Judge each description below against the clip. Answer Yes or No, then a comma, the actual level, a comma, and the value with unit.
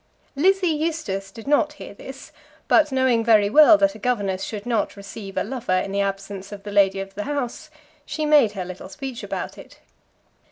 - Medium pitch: No, high, 225 Hz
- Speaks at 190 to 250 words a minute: Yes, average, 195 wpm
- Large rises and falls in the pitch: Yes, wide, 6.8 semitones